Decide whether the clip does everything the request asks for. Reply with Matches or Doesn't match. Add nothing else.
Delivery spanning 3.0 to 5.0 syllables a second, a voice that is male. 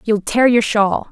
Doesn't match